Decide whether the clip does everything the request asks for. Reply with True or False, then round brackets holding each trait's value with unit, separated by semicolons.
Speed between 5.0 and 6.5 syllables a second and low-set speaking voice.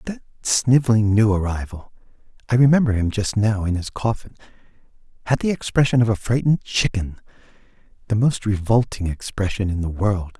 True (5.5 syllables/s; 110 Hz)